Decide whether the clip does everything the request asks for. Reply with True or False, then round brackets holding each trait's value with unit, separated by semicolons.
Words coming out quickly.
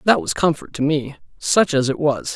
True (230 wpm)